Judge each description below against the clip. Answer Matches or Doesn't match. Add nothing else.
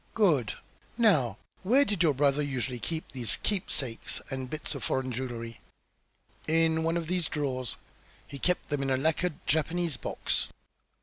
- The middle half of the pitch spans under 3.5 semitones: Doesn't match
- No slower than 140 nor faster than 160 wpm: Matches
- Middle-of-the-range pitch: Matches